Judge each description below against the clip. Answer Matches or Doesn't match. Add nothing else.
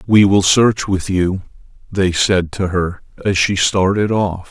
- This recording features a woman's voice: Doesn't match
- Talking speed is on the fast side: Doesn't match